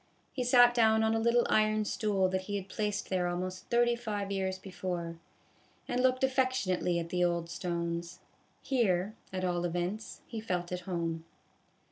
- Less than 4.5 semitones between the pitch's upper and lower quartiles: Yes, average, 4.0 semitones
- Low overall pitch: No, high, 190 Hz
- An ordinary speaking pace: Yes, average, 170 wpm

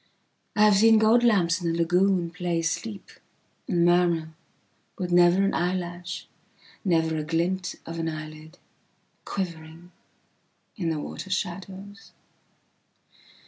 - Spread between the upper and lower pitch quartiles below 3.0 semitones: Yes, narrow, 2.6 semitones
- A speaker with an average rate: No, slow, 100 wpm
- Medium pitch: Yes, medium, 175 Hz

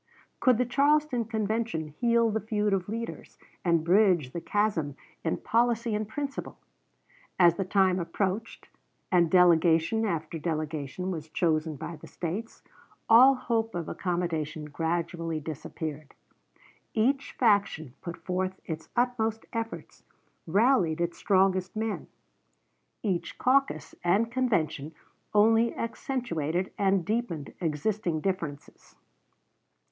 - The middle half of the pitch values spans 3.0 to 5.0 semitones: No, wide, 5.6 semitones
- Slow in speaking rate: Yes, slow, 115 wpm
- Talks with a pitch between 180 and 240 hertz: Yes, high, 190 Hz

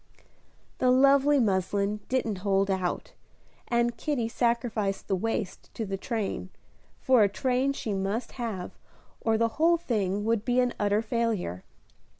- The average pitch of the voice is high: Yes, high, 225 Hz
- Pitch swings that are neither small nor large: Yes, average, 3.8 semitones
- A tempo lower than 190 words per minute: Yes, average, 145 wpm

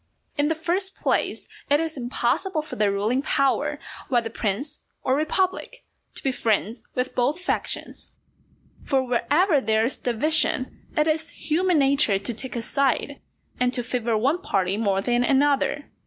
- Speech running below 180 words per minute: Yes, average, 155 wpm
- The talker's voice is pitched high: Yes, very high, 265 Hz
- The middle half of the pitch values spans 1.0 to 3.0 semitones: No, average, 4.8 semitones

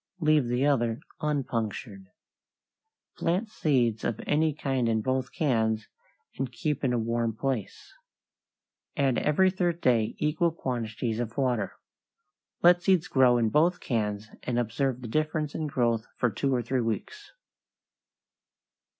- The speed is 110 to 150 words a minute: Yes, slow, 135 wpm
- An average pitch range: Yes, average, 4.8 semitones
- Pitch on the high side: No, low, 125 Hz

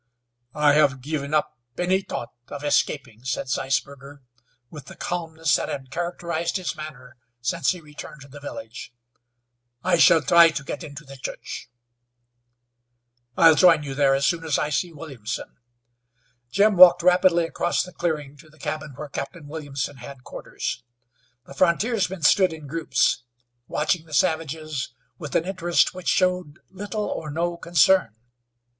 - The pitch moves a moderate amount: Yes, average, 3.7 semitones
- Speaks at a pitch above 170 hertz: No, medium, 155 Hz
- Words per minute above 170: No, average, 150 wpm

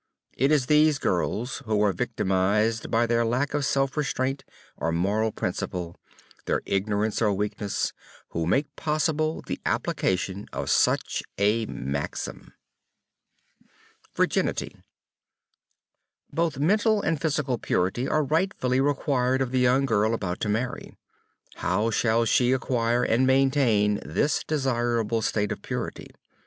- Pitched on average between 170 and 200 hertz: No, low, 120 Hz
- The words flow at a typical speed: No, slow, 125 wpm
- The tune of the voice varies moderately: Yes, average, 4.8 semitones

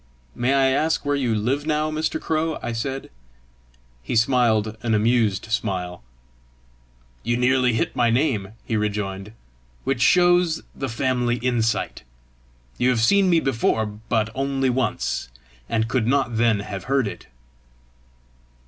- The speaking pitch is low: Yes, low, 120 Hz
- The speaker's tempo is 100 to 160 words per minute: Yes, average, 140 wpm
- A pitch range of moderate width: Yes, average, 3.7 semitones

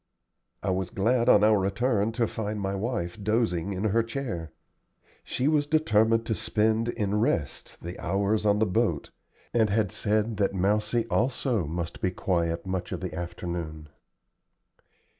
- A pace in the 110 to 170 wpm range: Yes, average, 155 wpm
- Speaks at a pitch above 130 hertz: No, low, 105 Hz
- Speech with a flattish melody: No, average, 3.6 semitones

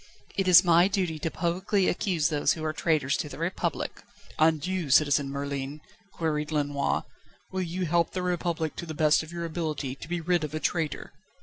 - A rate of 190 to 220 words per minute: Yes, average, 195 wpm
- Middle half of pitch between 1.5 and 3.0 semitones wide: Yes, average, 2.7 semitones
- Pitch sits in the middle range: Yes, medium, 160 Hz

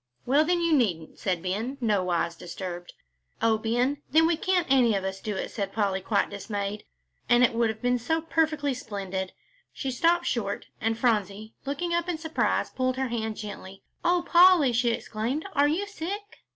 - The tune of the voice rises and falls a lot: Yes, wide, 7.4 semitones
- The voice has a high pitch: Yes, high, 240 Hz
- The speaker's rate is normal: Yes, average, 180 wpm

